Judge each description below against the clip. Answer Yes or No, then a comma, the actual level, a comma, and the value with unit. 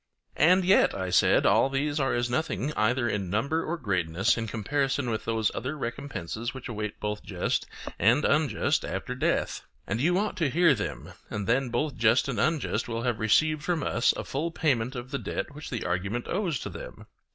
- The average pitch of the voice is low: Yes, low, 125 Hz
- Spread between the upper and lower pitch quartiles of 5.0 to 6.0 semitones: Yes, wide, 5.4 semitones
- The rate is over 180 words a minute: Yes, average, 195 wpm